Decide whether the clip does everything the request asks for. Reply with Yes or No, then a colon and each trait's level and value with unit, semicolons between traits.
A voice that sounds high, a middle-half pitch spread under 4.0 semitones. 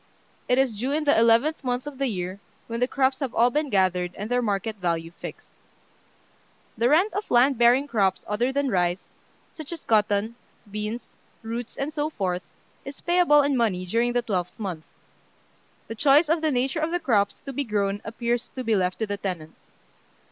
No: high, 235 Hz; average, 5.3 semitones